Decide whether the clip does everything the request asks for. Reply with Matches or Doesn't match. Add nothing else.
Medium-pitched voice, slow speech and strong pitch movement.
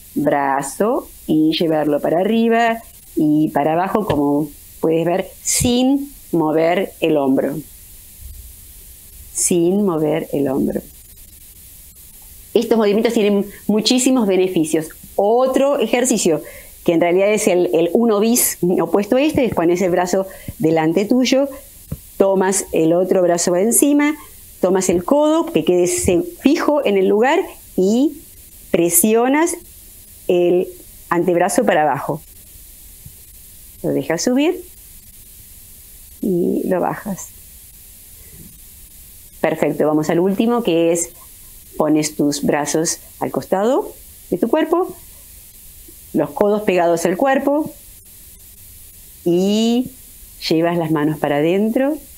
Matches